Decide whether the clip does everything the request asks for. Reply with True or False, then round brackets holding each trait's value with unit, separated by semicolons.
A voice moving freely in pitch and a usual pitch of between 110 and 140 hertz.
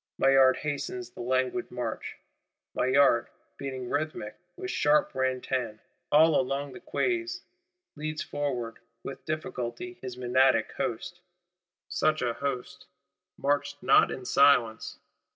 False (3.0 semitones; 135 Hz)